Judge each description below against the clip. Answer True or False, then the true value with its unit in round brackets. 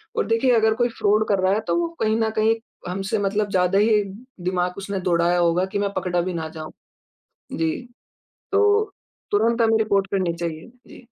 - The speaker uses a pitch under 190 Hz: False (200 Hz)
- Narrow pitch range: False (3.6 semitones)